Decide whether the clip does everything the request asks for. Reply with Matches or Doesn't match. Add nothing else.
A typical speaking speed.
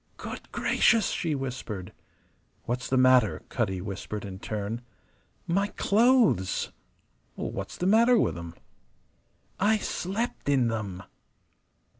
Doesn't match